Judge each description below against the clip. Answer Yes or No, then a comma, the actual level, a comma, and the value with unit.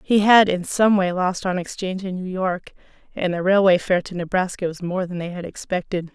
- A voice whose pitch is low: No, medium, 185 Hz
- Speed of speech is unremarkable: No, fast, 225 wpm